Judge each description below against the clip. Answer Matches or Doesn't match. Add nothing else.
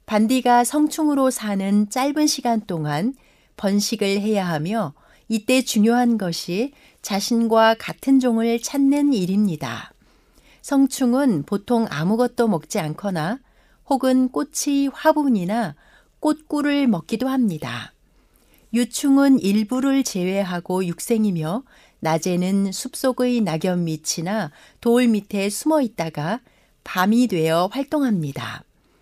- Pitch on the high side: Matches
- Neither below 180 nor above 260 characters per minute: Matches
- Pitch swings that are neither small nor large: Doesn't match